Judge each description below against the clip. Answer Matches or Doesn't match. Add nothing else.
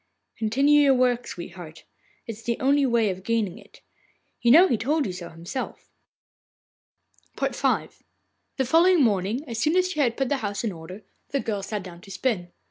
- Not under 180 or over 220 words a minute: Matches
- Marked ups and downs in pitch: Matches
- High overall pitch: Matches